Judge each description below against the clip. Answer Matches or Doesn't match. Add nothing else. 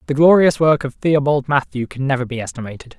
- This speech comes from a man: Matches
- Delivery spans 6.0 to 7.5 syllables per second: Matches